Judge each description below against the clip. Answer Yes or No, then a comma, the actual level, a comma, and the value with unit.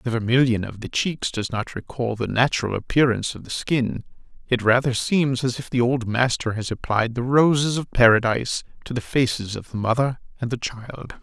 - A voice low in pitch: Yes, low, 120 Hz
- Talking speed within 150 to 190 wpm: No, average, 200 wpm